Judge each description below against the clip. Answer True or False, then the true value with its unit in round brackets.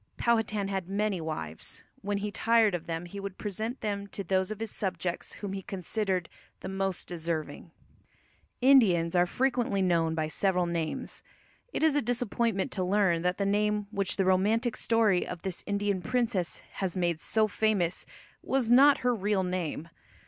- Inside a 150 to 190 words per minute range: True (170 wpm)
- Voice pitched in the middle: False (195 Hz)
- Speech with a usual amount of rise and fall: True (3.4 semitones)